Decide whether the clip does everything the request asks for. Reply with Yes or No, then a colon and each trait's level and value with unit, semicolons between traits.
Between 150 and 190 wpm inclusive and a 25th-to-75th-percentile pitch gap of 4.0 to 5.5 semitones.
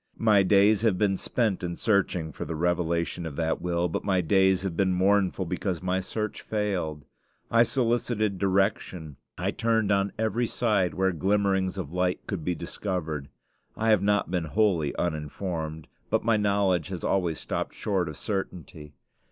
No: average, 165 wpm; average, 3.2 semitones